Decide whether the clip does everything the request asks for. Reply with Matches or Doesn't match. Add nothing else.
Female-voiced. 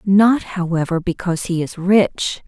Matches